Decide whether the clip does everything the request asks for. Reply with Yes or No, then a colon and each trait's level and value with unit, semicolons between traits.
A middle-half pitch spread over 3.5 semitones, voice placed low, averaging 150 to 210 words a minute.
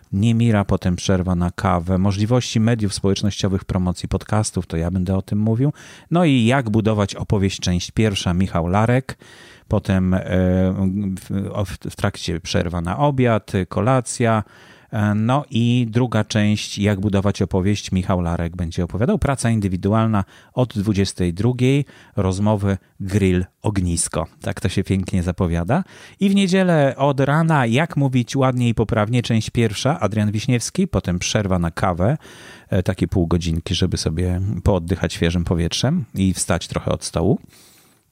No: average, 4.0 semitones; low, 100 Hz; average, 135 wpm